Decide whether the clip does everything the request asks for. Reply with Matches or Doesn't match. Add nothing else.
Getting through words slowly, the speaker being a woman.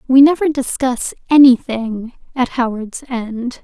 Matches